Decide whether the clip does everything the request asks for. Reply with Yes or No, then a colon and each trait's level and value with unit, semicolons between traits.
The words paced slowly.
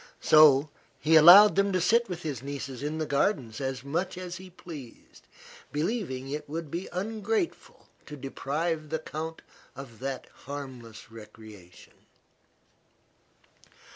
Yes: slow, 130 wpm